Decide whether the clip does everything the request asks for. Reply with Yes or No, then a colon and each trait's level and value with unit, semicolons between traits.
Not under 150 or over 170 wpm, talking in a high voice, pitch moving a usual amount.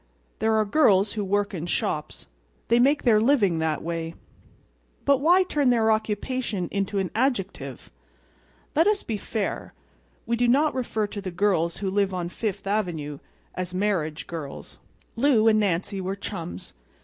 Yes: average, 160 wpm; high, 205 Hz; average, 4.7 semitones